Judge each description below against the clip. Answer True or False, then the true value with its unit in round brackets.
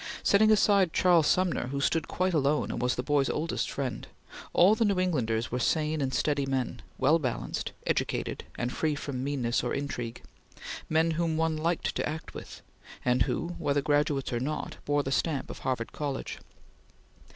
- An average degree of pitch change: True (3.8 semitones)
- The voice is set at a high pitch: False (145 Hz)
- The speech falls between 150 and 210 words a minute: True (175 wpm)